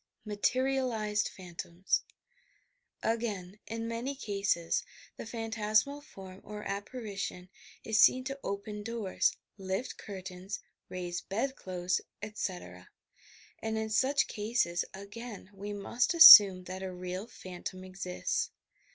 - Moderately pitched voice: No, high, 205 Hz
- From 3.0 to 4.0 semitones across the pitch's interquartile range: Yes, average, 3.5 semitones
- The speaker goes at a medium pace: No, slow, 115 wpm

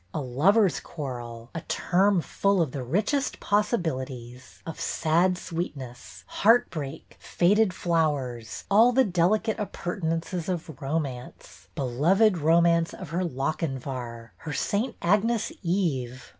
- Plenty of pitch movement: Yes, wide, 6.5 semitones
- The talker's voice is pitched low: No, medium, 165 Hz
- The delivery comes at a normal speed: No, slow, 115 wpm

